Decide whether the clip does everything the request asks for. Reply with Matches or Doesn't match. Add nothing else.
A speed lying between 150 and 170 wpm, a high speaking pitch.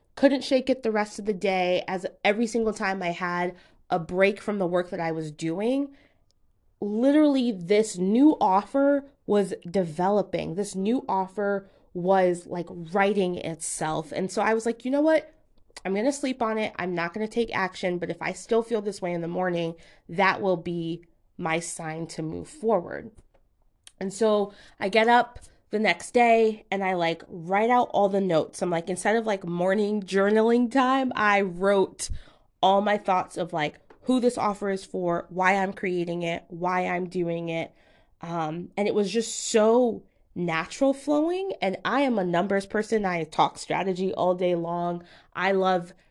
Doesn't match